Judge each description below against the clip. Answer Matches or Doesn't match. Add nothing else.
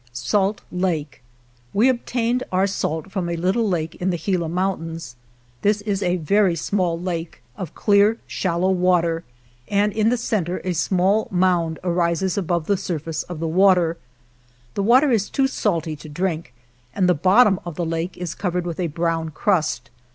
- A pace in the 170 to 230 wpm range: Matches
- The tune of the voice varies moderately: Matches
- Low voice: Doesn't match